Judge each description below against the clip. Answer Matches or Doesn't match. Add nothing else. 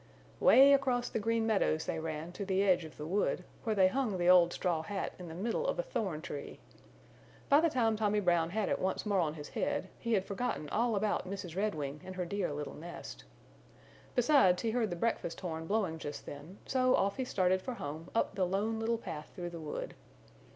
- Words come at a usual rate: Doesn't match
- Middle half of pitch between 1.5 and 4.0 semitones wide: Doesn't match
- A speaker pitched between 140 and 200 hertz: Matches